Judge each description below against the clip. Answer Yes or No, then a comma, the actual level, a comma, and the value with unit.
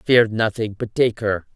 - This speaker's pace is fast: No, average, 195 wpm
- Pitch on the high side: No, low, 115 Hz